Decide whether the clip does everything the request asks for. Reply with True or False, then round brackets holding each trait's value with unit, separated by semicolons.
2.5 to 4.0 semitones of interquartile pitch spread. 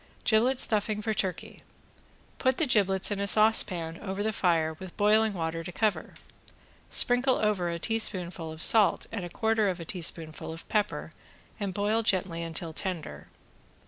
False (4.4 semitones)